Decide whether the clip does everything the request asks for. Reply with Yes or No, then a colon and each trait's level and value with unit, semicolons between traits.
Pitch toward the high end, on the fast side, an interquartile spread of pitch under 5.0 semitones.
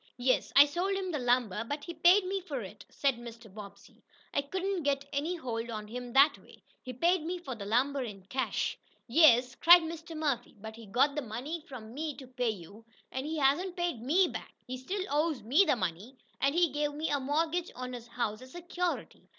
No: very high, 275 Hz; fast, 210 wpm; wide, 5.4 semitones